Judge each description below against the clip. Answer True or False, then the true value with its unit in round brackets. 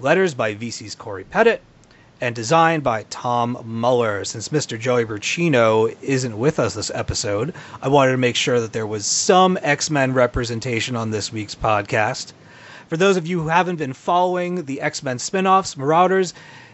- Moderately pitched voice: False (130 Hz)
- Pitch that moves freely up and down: True (6.1 semitones)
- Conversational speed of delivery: True (170 wpm)